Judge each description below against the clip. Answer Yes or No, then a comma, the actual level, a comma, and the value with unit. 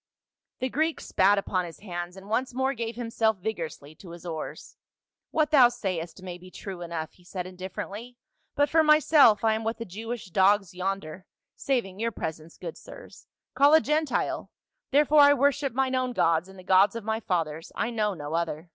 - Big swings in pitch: Yes, wide, 6.1 semitones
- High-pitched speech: Yes, high, 205 Hz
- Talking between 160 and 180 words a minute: No, average, 200 wpm